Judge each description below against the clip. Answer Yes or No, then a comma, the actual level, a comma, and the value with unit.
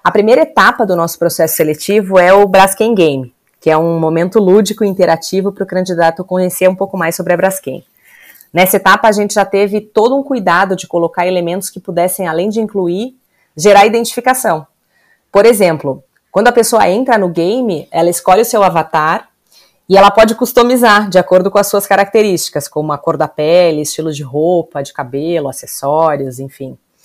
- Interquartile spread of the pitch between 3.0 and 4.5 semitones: Yes, average, 3.8 semitones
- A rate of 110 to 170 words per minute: No, average, 180 wpm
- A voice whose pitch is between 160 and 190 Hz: Yes, medium, 185 Hz